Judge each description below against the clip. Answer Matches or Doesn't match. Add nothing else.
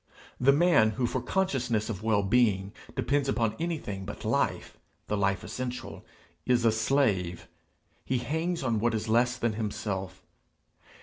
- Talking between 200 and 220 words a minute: Doesn't match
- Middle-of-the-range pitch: Doesn't match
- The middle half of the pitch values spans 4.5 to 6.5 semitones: Doesn't match